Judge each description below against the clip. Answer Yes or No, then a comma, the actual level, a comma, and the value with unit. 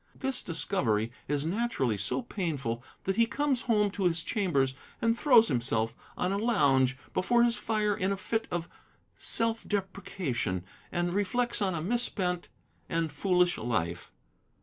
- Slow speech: No, average, 150 wpm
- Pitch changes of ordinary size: No, wide, 8.4 semitones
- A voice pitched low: No, medium, 185 Hz